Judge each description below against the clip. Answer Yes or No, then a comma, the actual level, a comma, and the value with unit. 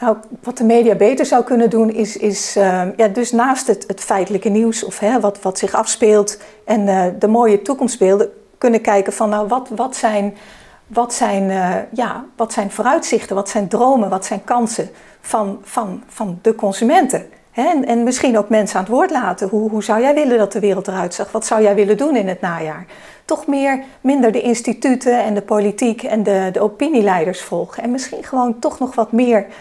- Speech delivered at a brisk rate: Yes, fast, 205 wpm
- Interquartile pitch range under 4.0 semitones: Yes, average, 2.9 semitones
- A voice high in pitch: Yes, high, 220 Hz